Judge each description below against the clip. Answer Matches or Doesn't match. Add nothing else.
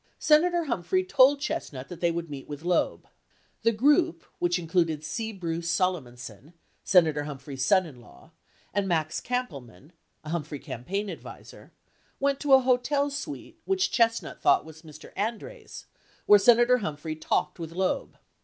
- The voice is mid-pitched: Matches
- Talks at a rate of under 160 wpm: Matches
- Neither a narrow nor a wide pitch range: Doesn't match